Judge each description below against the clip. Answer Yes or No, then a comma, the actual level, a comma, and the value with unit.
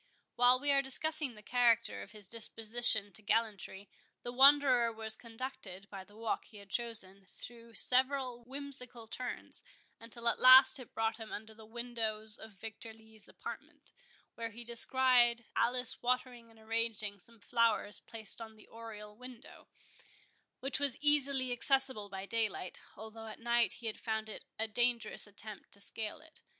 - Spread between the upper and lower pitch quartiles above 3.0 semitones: No, narrow, 2.4 semitones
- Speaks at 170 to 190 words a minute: No, average, 160 wpm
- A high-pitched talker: Yes, high, 230 Hz